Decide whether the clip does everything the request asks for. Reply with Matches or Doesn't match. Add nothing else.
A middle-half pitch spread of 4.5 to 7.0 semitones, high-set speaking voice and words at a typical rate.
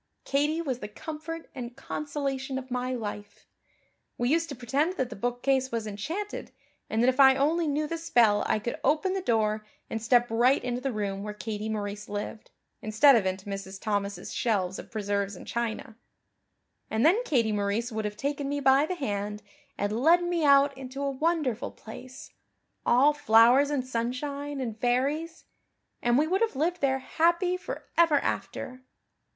Matches